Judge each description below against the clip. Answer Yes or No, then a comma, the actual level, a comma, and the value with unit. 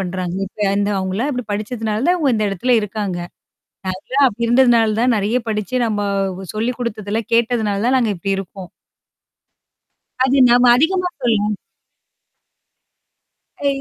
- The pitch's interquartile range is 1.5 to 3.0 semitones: No, average, 3.5 semitones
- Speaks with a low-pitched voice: No, high, 220 Hz